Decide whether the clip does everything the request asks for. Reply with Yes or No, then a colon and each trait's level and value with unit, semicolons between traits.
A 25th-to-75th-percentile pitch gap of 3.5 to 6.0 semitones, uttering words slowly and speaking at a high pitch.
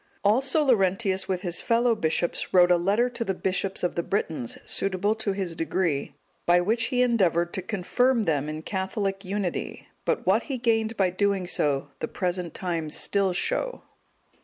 No: average, 3.9 semitones; average, 170 wpm; high, 195 Hz